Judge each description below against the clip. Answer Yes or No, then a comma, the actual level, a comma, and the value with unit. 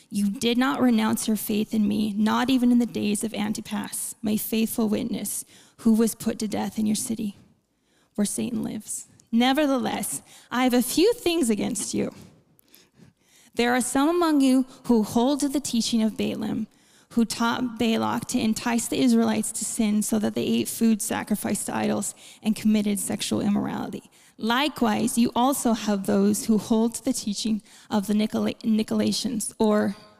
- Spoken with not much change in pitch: Yes, narrow, 2.1 semitones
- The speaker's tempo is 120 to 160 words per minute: No, average, 170 wpm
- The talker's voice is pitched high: Yes, high, 225 Hz